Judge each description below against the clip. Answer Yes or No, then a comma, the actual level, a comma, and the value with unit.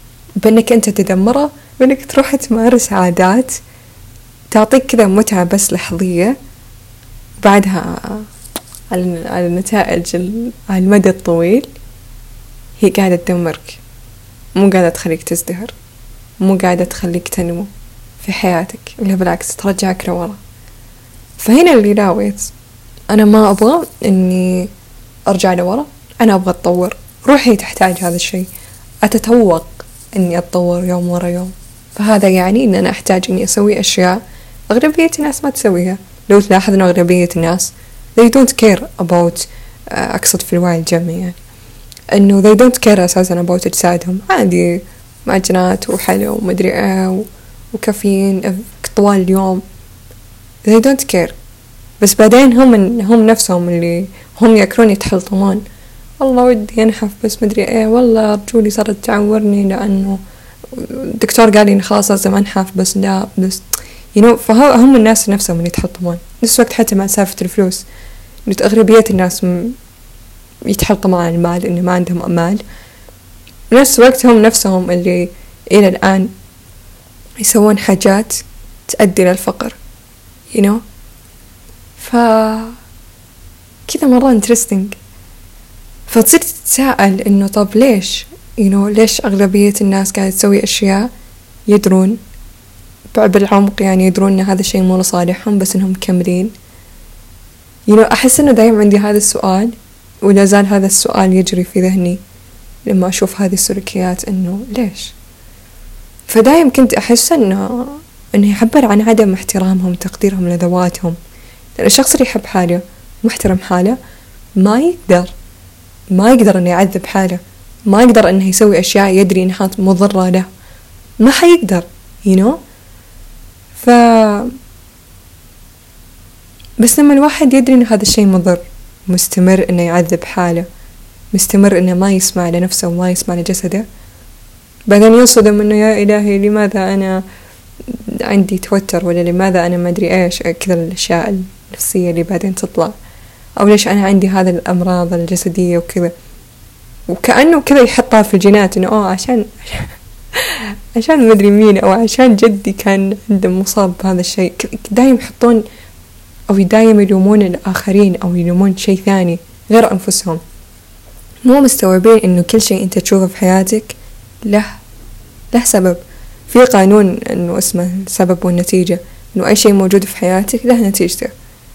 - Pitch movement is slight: No, average, 3.5 semitones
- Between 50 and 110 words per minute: No, average, 125 wpm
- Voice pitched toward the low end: No, high, 190 Hz